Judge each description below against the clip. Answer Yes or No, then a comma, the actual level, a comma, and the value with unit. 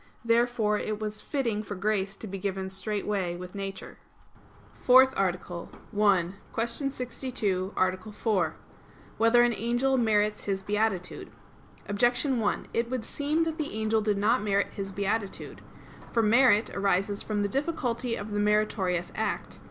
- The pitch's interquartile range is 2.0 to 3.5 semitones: Yes, average, 3.2 semitones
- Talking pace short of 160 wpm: Yes, average, 150 wpm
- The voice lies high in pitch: Yes, high, 210 Hz